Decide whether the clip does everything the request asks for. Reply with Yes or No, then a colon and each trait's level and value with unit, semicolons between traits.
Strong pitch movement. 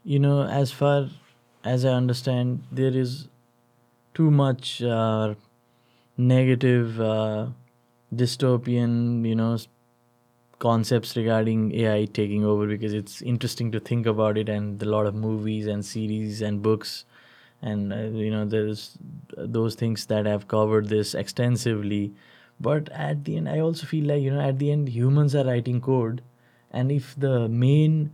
No: average, 2.9 semitones